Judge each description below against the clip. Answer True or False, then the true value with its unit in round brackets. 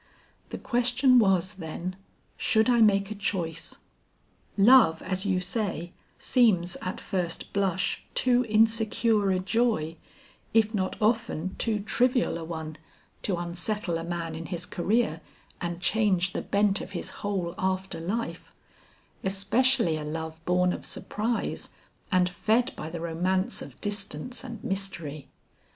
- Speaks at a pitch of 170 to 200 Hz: True (190 Hz)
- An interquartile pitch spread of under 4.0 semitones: False (4.3 semitones)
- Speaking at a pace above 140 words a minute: False (135 wpm)